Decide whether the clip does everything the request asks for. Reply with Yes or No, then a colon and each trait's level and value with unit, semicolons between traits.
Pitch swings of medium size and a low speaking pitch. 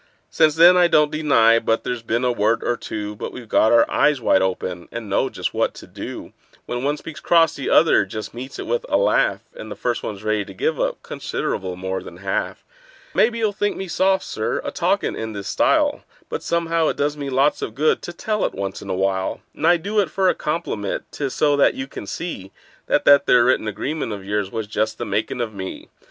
No: wide, 7.3 semitones; low, 125 Hz